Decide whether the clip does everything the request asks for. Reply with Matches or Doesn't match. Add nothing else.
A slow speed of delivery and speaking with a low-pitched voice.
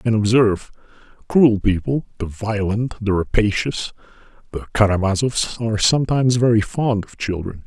Matches